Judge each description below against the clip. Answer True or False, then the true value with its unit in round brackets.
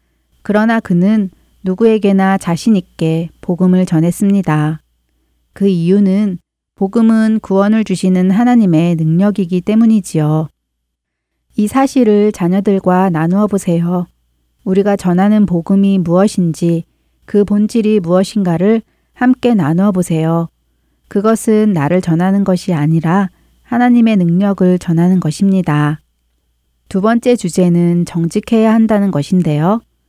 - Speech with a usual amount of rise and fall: True (3.9 semitones)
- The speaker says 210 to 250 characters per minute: False (270 characters per minute)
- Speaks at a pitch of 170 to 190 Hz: True (185 Hz)